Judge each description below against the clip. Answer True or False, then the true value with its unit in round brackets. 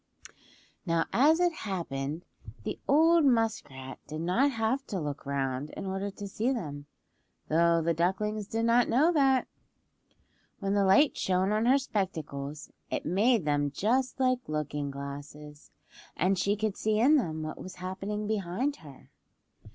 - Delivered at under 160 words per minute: True (150 wpm)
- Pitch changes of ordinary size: False (7.1 semitones)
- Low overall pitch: False (195 Hz)